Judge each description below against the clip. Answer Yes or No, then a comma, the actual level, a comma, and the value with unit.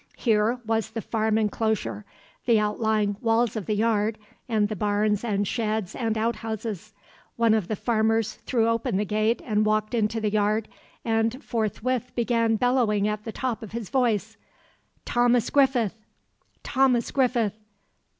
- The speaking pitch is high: Yes, high, 220 Hz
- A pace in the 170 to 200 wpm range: No, average, 150 wpm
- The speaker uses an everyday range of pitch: No, narrow, 1.8 semitones